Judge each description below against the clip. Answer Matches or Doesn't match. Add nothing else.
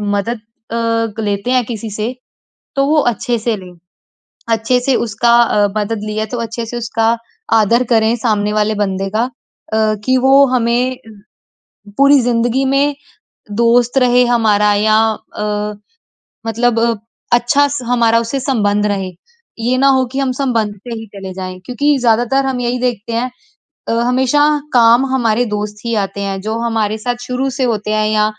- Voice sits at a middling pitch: Doesn't match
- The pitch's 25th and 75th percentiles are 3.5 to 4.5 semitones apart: Doesn't match